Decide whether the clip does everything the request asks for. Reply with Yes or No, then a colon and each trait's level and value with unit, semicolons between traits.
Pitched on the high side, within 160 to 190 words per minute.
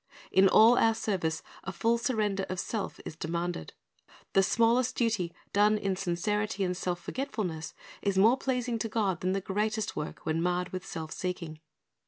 Yes: high, 195 Hz; average, 170 wpm